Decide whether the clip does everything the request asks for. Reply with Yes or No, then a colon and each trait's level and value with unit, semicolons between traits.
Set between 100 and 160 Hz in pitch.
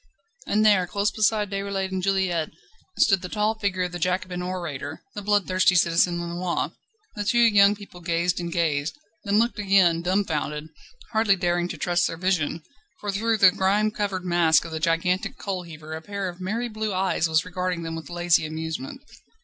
No: medium, 185 Hz